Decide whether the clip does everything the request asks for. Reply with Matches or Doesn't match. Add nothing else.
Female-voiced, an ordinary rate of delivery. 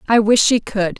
Doesn't match